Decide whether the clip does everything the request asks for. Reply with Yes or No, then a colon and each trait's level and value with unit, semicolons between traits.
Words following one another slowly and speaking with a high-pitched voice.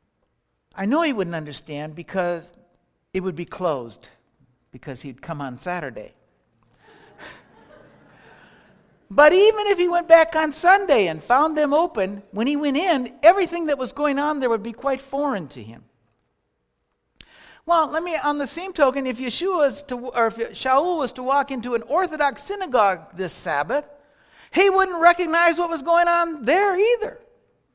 No: average, 160 wpm; very high, 265 Hz